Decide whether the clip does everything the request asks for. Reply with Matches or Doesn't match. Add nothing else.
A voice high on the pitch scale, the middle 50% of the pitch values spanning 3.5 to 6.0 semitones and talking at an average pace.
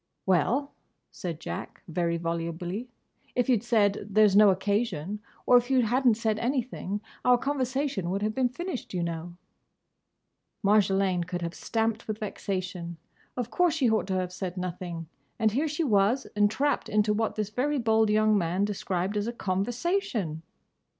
Matches